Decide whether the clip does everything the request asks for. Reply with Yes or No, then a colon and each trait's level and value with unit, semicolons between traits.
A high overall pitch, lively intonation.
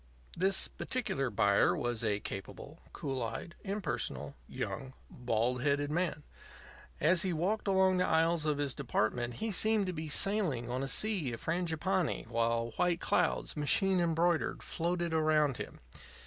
No: medium, 155 Hz; wide, 6.5 semitones